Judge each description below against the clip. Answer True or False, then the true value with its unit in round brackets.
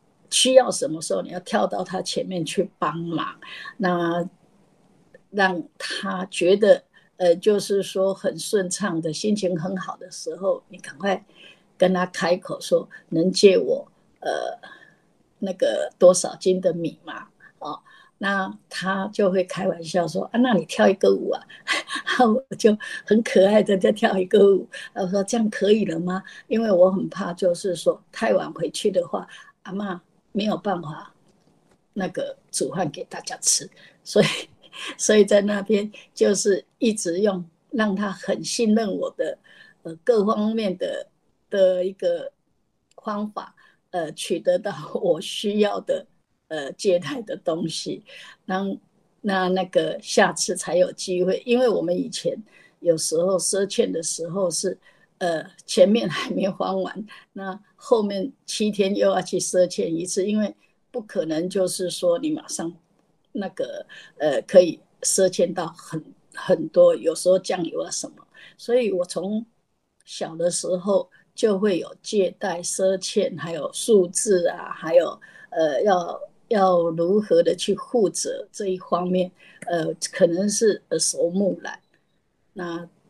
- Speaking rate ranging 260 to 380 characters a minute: False (205 characters per minute)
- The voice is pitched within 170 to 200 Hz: True (195 Hz)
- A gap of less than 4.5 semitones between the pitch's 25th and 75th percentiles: True (3.2 semitones)